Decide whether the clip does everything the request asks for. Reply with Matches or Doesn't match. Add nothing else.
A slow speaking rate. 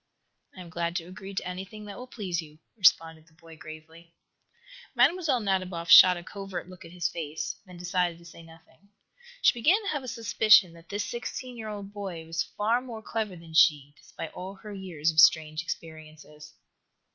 Doesn't match